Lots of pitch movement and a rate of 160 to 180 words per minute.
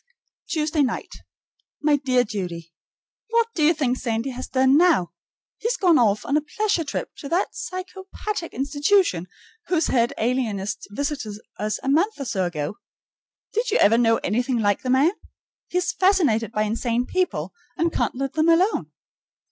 Yes: wide, 7.0 semitones; average, 165 wpm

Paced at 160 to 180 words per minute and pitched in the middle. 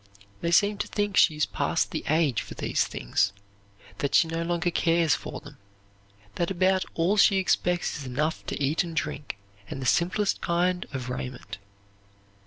Yes: average, 175 wpm; medium, 170 Hz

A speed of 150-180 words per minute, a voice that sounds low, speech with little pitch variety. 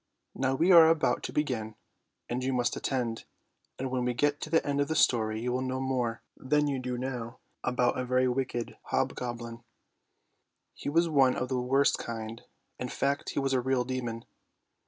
No: average, 190 wpm; low, 130 Hz; narrow, 2.1 semitones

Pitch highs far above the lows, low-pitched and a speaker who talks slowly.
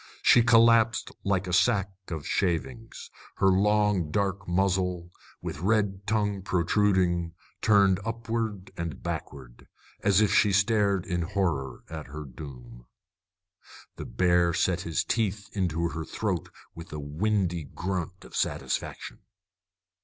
No: average, 3.5 semitones; very low, 95 Hz; slow, 125 wpm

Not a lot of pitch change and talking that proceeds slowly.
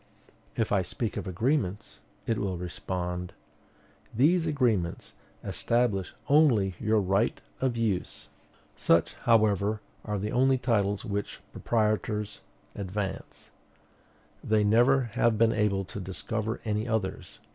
No: average, 3.2 semitones; slow, 115 wpm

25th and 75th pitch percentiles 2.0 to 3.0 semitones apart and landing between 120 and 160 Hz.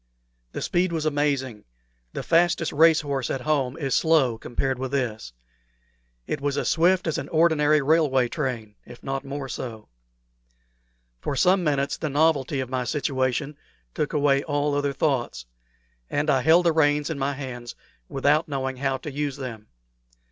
Yes: average, 2.7 semitones; medium, 140 Hz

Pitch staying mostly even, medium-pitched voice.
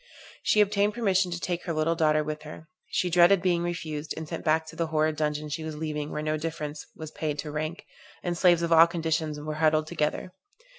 Yes: narrow, 2.1 semitones; medium, 160 Hz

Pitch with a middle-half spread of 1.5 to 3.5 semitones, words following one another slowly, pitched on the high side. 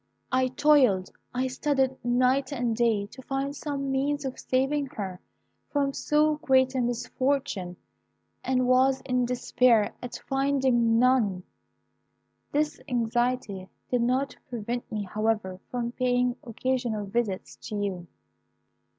Yes: average, 2.9 semitones; slow, 125 wpm; very high, 250 Hz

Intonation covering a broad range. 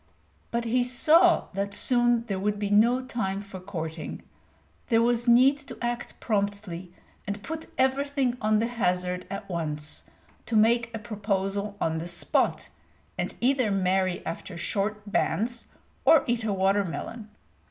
No: average, 3.9 semitones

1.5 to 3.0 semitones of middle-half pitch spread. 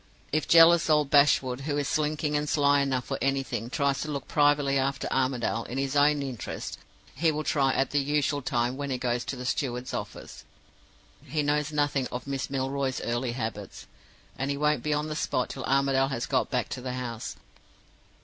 Yes: narrow, 2.4 semitones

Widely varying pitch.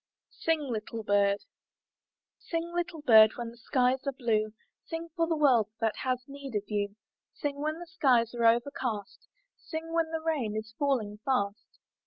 Yes: wide, 6.1 semitones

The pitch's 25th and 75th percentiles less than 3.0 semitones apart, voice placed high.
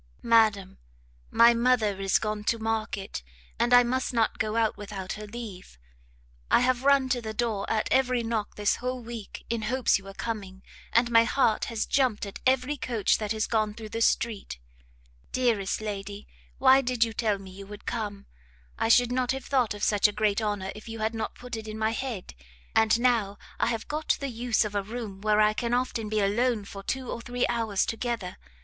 Yes: narrow, 2.6 semitones; high, 225 Hz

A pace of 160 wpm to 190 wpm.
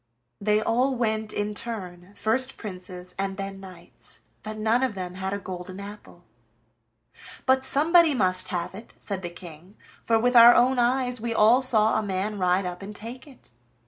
Yes: average, 175 wpm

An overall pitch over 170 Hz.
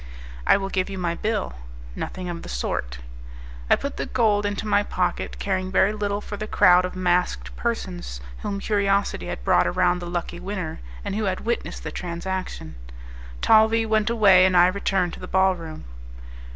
Yes: high, 190 Hz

